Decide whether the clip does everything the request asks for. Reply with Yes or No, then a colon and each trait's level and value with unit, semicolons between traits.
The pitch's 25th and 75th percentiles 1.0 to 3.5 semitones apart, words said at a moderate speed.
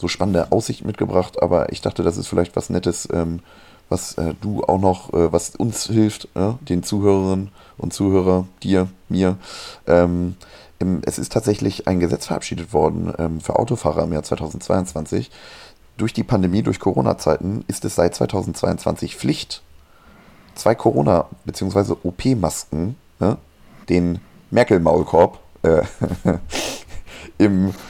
No: average, 2.7 semitones; slow, 120 wpm